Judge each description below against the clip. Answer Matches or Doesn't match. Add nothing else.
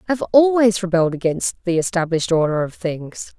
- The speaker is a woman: Matches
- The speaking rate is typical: Matches